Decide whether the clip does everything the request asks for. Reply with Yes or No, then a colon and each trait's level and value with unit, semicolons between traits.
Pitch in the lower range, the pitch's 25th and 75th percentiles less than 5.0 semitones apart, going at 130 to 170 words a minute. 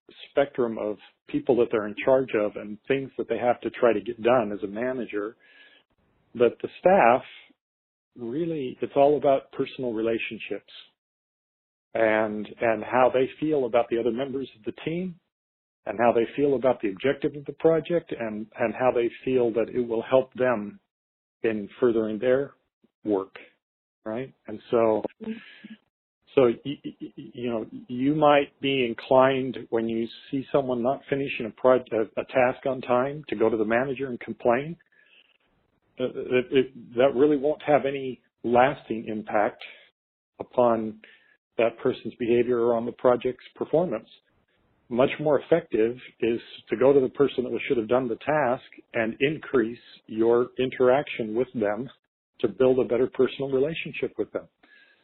Yes: low, 125 Hz; average, 3.1 semitones; average, 155 wpm